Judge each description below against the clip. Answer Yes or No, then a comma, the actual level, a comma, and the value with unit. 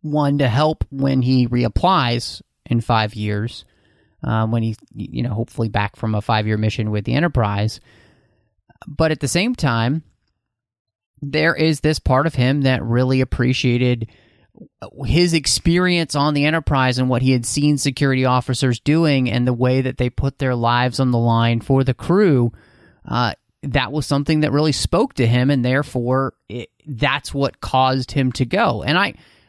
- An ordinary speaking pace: Yes, average, 175 wpm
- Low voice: Yes, low, 130 Hz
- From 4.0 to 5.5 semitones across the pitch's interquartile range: No, average, 3.6 semitones